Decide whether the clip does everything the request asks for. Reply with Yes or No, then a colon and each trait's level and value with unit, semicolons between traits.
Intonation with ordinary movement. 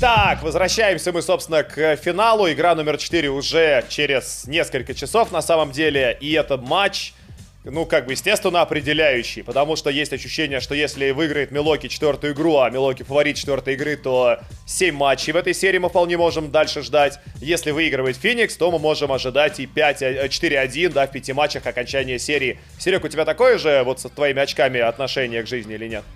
Yes: average, 3.5 semitones